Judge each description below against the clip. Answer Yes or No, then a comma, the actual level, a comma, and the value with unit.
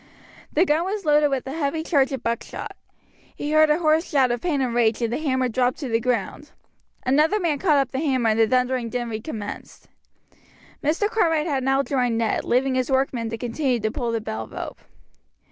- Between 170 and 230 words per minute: Yes, fast, 205 wpm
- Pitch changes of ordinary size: Yes, average, 4.1 semitones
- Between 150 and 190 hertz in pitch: No, very high, 265 Hz